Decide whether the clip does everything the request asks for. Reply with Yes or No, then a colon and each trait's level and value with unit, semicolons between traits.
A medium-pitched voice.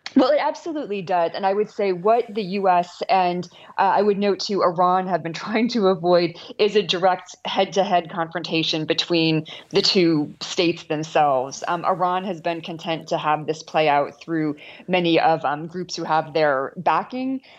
Yes: medium, 180 Hz